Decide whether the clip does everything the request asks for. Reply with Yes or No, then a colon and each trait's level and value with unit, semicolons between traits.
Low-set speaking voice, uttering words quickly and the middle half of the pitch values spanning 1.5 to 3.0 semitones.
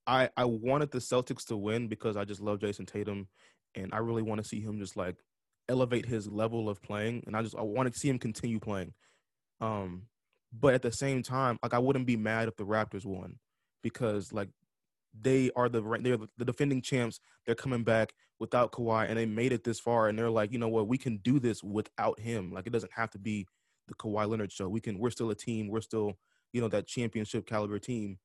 Yes: low, 115 Hz; fast, 230 wpm; narrow, 2.5 semitones